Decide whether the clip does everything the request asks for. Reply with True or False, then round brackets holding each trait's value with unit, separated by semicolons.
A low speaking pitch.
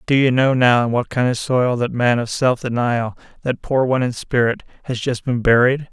True (125 Hz)